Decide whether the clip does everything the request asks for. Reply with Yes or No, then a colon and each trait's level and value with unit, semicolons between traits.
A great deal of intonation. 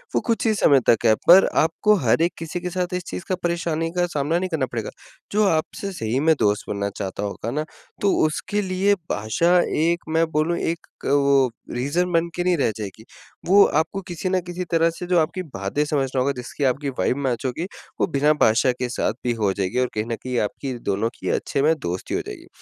Yes: wide, 6.2 semitones